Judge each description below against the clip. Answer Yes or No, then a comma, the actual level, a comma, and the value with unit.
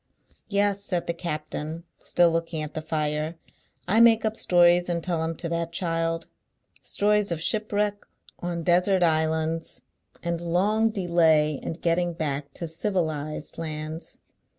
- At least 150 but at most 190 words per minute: No, average, 140 wpm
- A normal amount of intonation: No, narrow, 2.3 semitones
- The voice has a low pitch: No, medium, 170 Hz